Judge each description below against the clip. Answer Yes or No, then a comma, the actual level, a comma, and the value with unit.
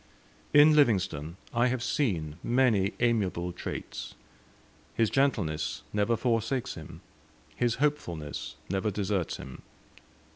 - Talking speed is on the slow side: Yes, slow, 105 wpm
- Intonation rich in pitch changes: Yes, wide, 5.9 semitones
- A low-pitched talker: Yes, low, 110 Hz